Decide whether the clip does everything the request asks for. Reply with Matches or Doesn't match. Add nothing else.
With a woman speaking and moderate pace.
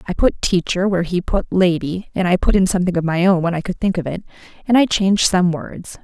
Doesn't match